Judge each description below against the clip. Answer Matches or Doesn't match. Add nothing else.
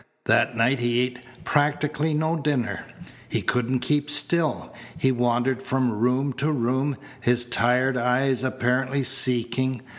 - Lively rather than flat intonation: Doesn't match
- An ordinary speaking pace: Doesn't match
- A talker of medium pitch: Doesn't match